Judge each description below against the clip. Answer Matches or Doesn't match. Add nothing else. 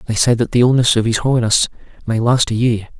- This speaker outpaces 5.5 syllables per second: Matches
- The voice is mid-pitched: Doesn't match